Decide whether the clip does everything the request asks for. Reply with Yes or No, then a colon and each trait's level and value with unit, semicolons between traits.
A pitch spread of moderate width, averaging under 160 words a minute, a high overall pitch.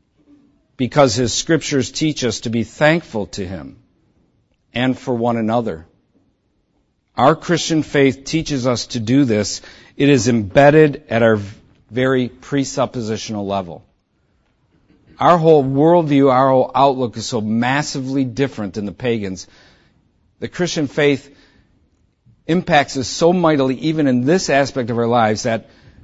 No: average, 3.8 semitones; slow, 135 wpm; low, 130 Hz